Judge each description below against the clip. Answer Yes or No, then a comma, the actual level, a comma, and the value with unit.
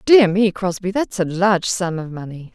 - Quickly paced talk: Yes, fast, 210 wpm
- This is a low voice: No, high, 190 Hz